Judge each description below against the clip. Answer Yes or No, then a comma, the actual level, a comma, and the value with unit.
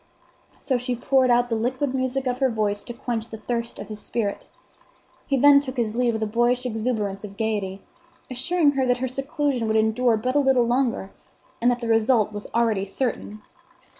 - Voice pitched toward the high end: Yes, high, 240 Hz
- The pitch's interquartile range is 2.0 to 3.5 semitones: Yes, average, 2.9 semitones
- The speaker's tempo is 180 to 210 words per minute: Yes, average, 195 wpm